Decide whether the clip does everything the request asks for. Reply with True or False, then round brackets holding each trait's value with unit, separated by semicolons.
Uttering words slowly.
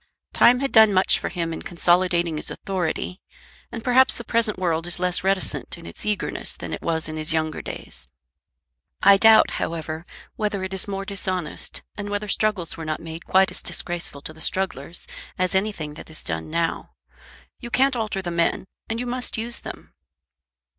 False (185 wpm)